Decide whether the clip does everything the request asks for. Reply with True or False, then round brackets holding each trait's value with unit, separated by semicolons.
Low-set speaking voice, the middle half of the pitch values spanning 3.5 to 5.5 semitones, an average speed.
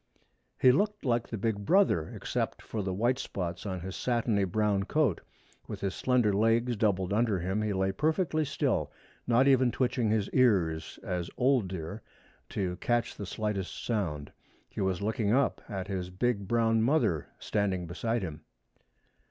True (105 Hz; 4.3 semitones; 160 wpm)